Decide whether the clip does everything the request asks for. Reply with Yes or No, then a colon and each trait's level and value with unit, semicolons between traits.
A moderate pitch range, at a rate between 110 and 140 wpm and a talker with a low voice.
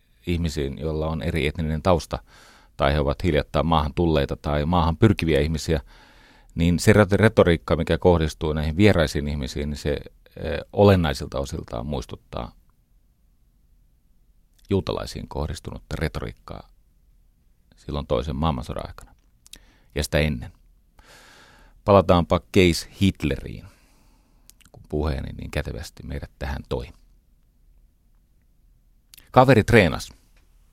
No: average, 3.1 semitones; average, 100 wpm; very low, 80 Hz